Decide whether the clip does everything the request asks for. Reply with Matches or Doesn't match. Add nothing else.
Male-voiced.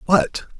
Matches